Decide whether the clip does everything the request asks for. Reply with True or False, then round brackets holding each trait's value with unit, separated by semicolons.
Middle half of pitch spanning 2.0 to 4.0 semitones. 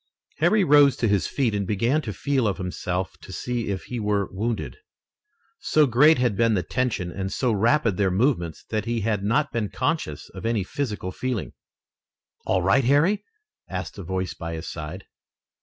False (5.3 semitones)